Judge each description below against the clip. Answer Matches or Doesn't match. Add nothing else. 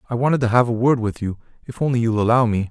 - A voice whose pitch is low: Matches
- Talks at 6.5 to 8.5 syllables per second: Matches